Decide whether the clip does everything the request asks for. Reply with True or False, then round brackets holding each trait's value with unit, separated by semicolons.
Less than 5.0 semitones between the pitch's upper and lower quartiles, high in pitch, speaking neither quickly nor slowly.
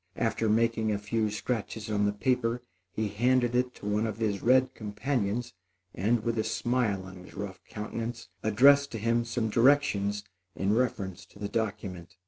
False (2.8 semitones; 110 Hz; 170 wpm)